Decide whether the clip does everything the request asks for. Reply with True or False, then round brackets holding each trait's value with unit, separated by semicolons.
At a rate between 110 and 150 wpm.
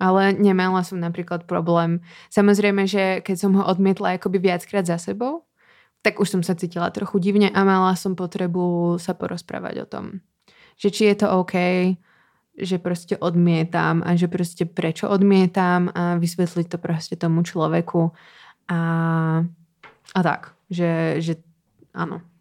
True (145 wpm)